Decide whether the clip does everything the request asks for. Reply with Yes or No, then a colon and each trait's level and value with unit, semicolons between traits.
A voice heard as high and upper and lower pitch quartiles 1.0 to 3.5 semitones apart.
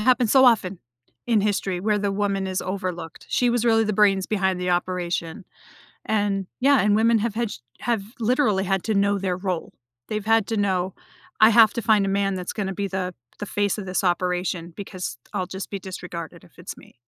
Yes: high, 200 Hz; average, 2.8 semitones